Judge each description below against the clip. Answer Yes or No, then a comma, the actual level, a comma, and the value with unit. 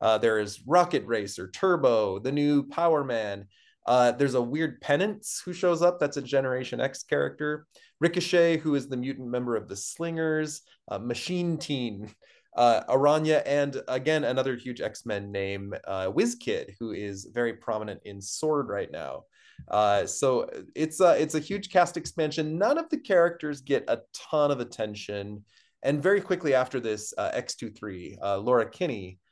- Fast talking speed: No, average, 165 wpm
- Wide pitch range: Yes, wide, 6.8 semitones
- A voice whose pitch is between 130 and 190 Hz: Yes, medium, 140 Hz